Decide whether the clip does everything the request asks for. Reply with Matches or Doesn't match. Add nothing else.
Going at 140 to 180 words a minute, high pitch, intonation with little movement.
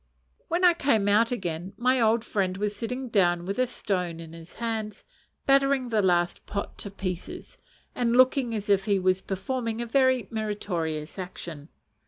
Doesn't match